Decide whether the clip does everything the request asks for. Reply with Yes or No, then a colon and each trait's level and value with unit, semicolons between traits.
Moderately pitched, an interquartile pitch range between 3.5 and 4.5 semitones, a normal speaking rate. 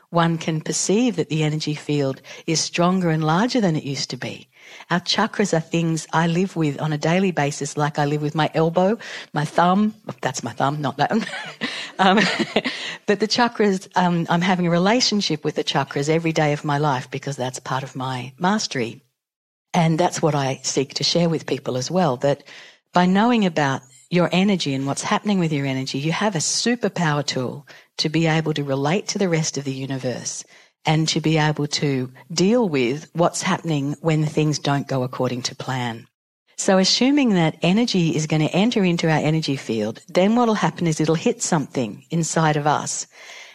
Yes: medium, 160 Hz; average, 3.8 semitones; average, 195 wpm